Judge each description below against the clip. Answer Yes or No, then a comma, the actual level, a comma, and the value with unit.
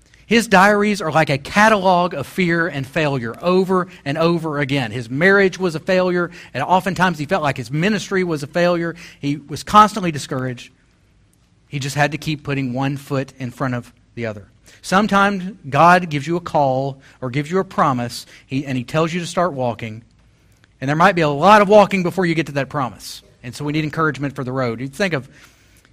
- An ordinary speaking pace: No, fast, 210 wpm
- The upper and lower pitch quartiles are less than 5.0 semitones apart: No, wide, 5.6 semitones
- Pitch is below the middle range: No, medium, 145 Hz